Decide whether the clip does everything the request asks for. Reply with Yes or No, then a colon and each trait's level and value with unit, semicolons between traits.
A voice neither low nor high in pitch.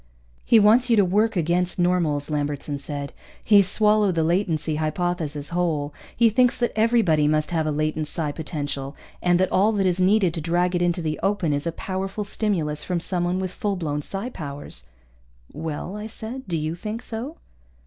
Yes: medium, 175 Hz